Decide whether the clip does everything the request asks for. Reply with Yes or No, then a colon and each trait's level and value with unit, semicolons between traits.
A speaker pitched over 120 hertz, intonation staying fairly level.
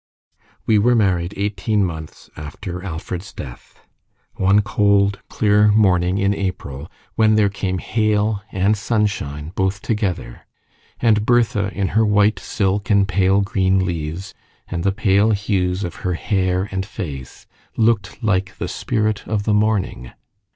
No: low, 100 Hz; narrow, 2.3 semitones